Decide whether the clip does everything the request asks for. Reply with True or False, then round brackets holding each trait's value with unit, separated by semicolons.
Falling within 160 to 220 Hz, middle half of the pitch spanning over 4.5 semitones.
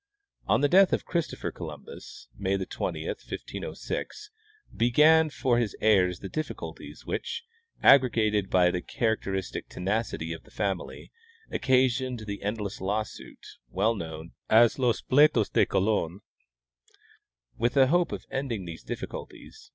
False (110 Hz; 5.3 semitones)